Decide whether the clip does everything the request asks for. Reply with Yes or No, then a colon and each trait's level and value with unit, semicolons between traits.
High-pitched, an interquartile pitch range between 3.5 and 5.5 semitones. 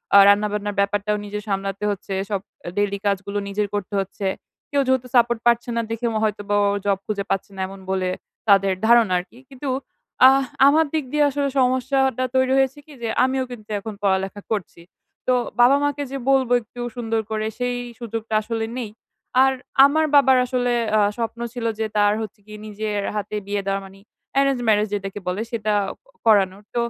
Yes: high, 220 Hz; average, 3.8 semitones